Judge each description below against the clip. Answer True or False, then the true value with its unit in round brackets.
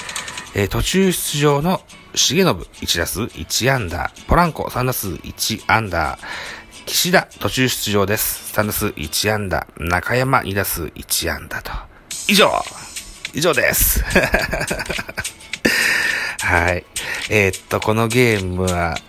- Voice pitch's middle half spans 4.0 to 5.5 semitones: True (5.2 semitones)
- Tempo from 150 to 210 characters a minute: True (205 characters per minute)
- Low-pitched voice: True (105 Hz)